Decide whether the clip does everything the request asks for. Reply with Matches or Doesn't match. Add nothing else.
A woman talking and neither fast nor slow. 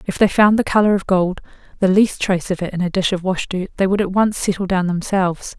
Doesn't match